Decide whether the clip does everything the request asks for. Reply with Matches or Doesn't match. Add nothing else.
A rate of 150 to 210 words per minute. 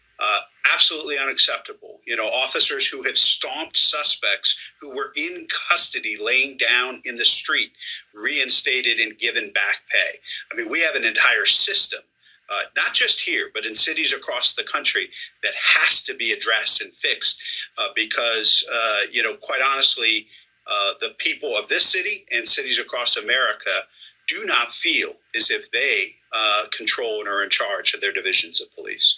Matches